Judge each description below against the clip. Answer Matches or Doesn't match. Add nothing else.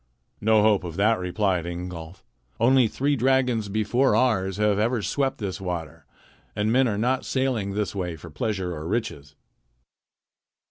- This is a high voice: Doesn't match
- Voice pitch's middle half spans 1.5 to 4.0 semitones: Doesn't match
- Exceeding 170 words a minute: Doesn't match